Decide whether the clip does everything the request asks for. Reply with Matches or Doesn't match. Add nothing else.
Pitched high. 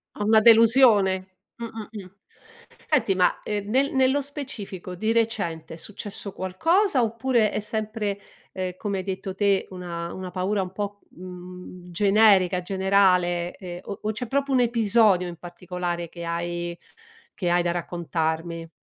Matches